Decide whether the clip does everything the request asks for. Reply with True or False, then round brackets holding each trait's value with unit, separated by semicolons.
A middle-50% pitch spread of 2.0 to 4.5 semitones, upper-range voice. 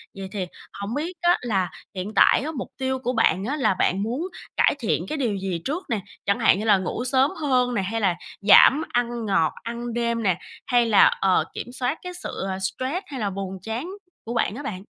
False (5.1 semitones; 230 Hz)